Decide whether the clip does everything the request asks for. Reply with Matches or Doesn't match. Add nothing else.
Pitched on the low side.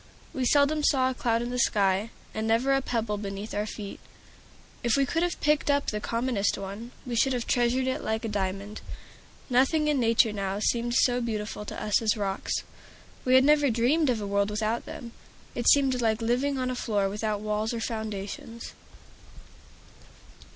Doesn't match